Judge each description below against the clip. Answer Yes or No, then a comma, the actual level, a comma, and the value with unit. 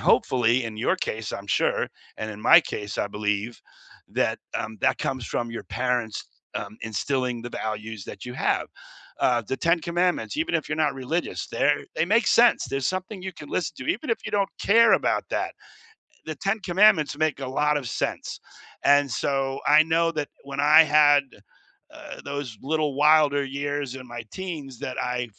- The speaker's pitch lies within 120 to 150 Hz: Yes, medium, 140 Hz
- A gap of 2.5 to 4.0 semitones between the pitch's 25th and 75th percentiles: No, average, 4.8 semitones